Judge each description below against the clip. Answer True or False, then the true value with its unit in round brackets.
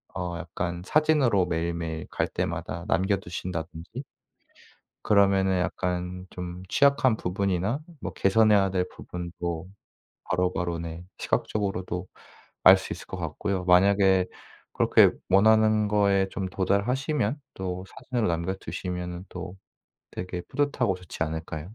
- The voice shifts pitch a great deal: False (2.4 semitones)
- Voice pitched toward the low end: True (95 Hz)